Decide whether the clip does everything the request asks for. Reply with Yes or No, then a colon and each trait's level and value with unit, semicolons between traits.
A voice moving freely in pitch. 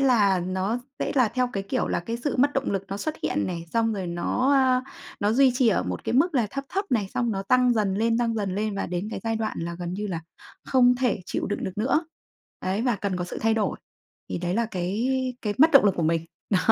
No: average, 4.7 semitones